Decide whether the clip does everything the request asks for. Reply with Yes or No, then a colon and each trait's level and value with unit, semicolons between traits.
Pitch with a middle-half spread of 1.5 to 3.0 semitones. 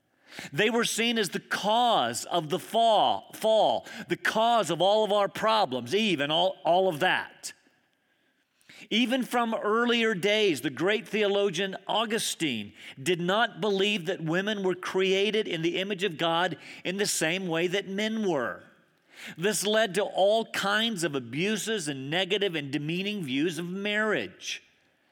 No: average, 3.4 semitones